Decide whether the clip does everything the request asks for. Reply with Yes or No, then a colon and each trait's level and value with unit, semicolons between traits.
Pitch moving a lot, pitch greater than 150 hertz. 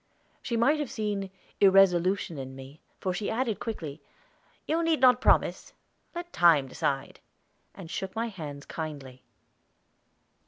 Yes: wide, 7.6 semitones; high, 190 Hz